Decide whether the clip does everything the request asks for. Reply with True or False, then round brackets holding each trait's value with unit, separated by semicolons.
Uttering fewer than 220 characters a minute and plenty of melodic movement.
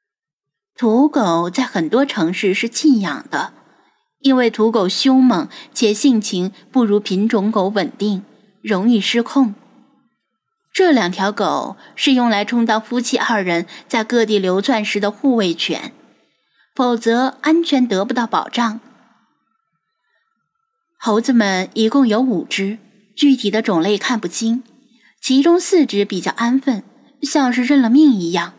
False (195 characters per minute; 4.6 semitones)